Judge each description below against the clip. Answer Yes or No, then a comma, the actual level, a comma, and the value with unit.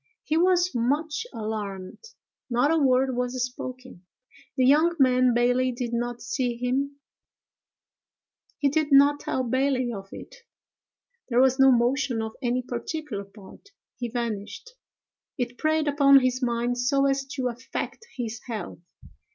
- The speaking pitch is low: No, very high, 255 Hz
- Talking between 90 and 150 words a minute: Yes, average, 140 wpm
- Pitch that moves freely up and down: No, average, 2.7 semitones